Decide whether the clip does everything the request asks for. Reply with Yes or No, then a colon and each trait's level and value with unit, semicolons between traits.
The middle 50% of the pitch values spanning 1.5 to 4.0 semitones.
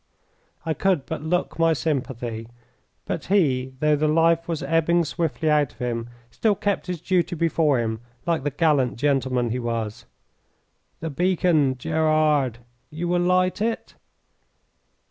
No: average, 4.6 semitones